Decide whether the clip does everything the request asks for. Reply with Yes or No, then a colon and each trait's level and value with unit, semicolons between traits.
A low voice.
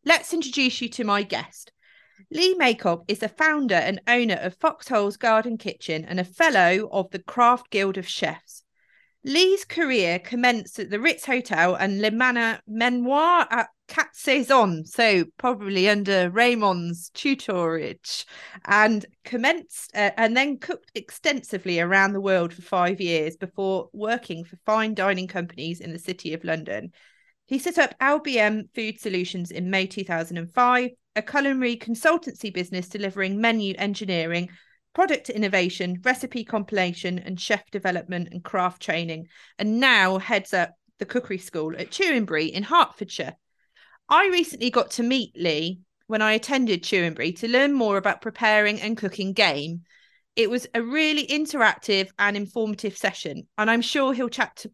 No: high, 210 Hz